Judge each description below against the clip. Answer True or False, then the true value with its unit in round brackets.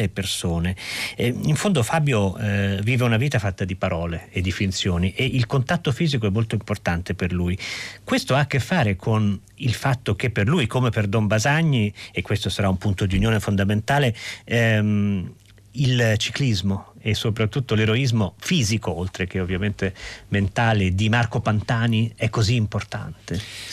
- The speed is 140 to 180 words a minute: True (160 wpm)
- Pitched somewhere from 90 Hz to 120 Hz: True (110 Hz)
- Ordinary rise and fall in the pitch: True (3.4 semitones)